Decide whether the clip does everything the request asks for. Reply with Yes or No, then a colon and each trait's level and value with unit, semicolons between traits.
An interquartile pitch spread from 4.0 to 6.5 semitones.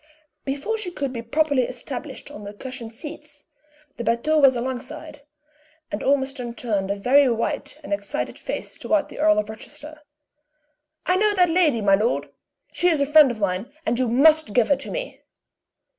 Yes: average, 5.0 semitones